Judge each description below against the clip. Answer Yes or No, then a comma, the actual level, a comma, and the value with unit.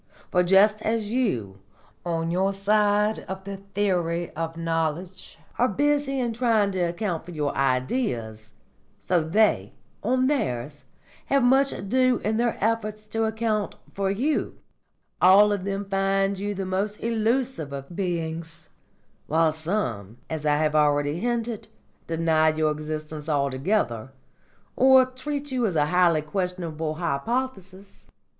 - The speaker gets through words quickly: No, slow, 135 wpm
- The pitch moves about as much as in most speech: No, wide, 5.7 semitones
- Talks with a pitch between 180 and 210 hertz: Yes, high, 190 Hz